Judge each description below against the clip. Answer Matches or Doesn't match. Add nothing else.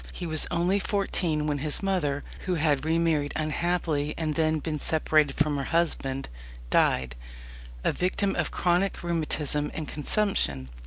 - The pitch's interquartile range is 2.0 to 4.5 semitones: Matches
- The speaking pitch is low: Doesn't match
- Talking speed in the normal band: Matches